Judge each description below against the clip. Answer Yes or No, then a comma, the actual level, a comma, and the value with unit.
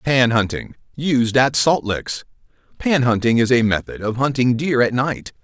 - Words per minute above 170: No, average, 165 wpm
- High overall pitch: No, low, 125 Hz